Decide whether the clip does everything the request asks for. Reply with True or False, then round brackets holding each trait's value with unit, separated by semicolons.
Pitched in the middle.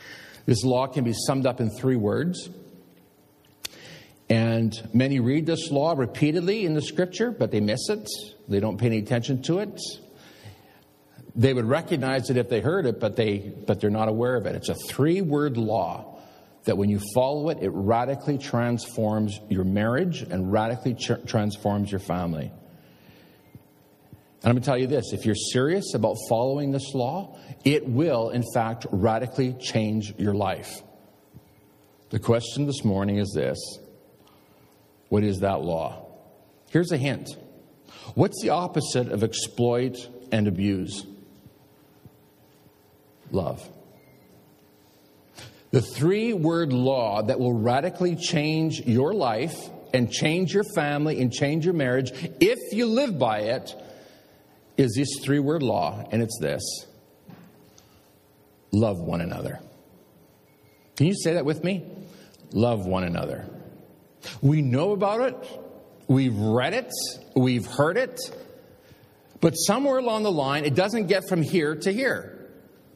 False (125 Hz)